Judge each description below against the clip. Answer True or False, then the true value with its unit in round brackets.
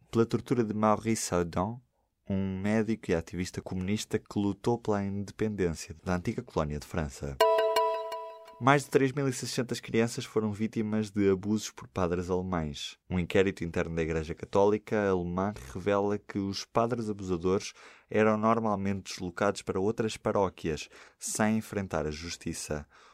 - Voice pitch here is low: True (105 Hz)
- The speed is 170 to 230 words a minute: False (135 wpm)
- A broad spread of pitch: False (3.4 semitones)